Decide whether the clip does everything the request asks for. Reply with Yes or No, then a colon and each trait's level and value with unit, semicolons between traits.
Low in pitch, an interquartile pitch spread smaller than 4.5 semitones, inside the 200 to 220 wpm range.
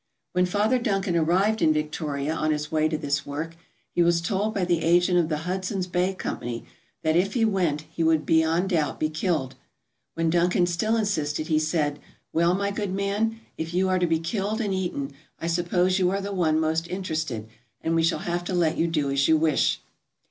No: medium, 170 Hz; average, 3.2 semitones; fast, 205 wpm